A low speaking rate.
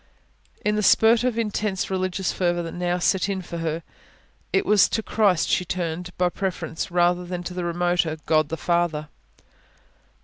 No: average, 170 wpm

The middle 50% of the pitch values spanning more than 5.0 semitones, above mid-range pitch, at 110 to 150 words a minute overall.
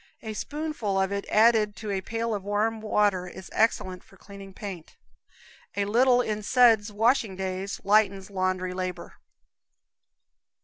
No: average, 2.7 semitones; high, 205 Hz; average, 140 wpm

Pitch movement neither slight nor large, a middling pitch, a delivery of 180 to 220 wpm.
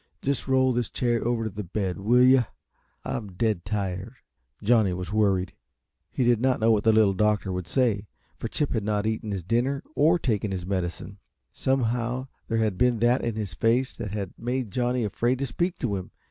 No: average, 3.7 semitones; low, 110 Hz; average, 200 wpm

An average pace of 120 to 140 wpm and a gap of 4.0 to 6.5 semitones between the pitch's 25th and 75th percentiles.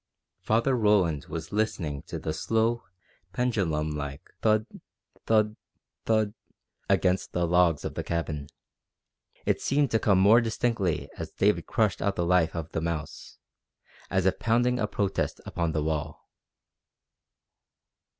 Yes: slow, 135 wpm; wide, 5.4 semitones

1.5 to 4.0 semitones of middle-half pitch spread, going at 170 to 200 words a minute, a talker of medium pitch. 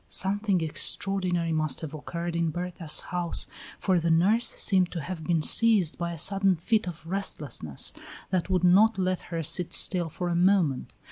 Yes: narrow, 2.6 semitones; average, 175 wpm; medium, 175 Hz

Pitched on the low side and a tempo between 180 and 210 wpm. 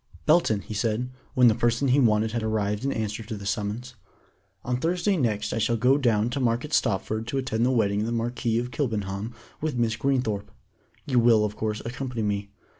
Yes: low, 115 Hz; average, 200 wpm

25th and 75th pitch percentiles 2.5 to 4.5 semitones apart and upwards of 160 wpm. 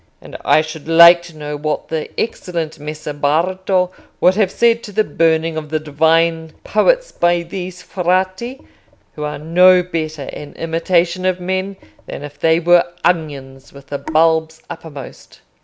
No: average, 2.8 semitones; average, 155 wpm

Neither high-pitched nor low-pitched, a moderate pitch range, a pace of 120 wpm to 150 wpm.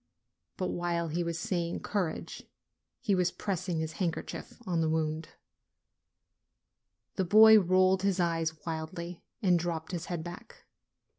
No: medium, 175 Hz; narrow, 2.2 semitones; average, 145 wpm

